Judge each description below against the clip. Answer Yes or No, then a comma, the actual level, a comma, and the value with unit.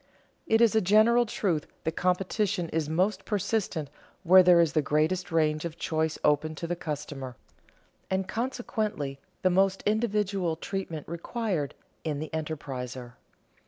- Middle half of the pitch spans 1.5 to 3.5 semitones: No, average, 4.7 semitones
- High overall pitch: No, medium, 170 Hz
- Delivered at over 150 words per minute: No, average, 145 wpm